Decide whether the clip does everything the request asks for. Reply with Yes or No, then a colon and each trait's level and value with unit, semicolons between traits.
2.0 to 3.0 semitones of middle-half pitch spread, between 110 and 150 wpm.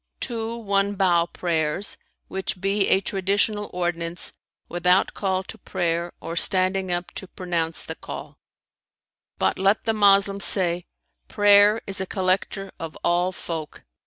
Yes: narrow, 2.4 semitones; slow, 135 wpm